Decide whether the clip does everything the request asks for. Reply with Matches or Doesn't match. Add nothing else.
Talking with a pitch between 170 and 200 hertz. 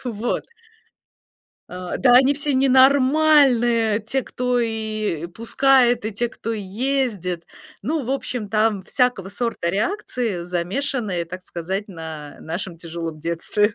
Doesn't match